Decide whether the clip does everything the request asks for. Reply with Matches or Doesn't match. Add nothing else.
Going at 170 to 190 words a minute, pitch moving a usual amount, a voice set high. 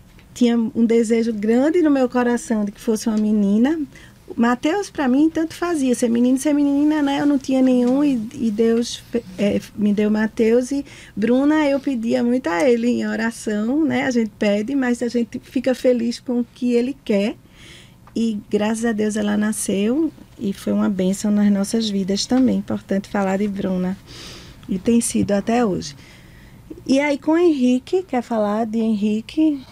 Matches